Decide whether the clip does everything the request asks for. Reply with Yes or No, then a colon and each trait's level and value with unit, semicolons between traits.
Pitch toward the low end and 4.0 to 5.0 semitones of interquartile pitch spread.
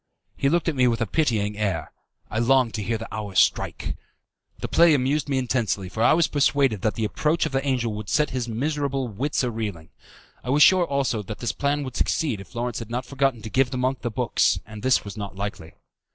Yes: low, 125 Hz; average, 4.4 semitones